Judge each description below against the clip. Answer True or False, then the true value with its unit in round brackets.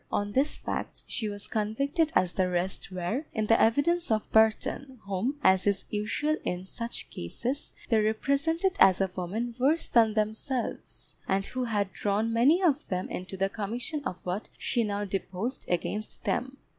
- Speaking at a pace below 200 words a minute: True (170 wpm)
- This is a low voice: False (220 Hz)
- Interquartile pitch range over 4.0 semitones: True (5.2 semitones)